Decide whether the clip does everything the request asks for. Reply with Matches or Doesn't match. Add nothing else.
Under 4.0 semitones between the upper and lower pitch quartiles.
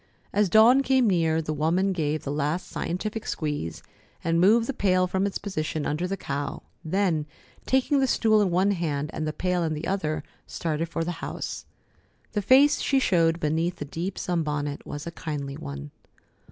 Doesn't match